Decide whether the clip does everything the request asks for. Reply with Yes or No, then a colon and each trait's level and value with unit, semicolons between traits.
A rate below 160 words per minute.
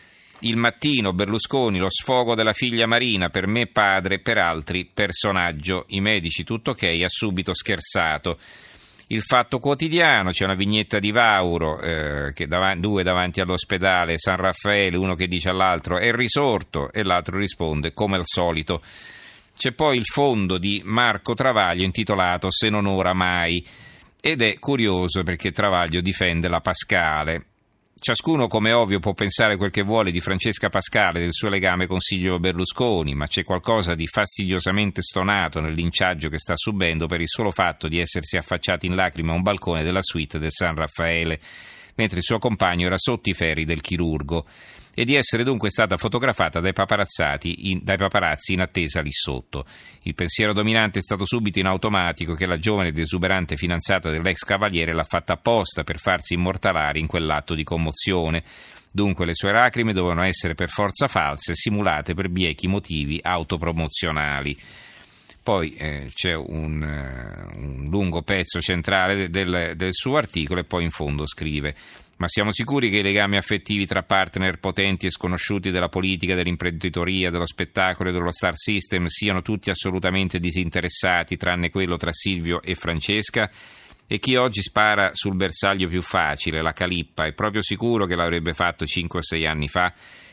No: average, 165 wpm